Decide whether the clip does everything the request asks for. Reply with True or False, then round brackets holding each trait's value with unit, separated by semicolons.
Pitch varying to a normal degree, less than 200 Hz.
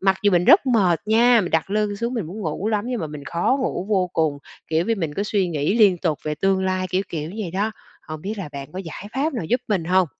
True (4.6 semitones; 190 Hz)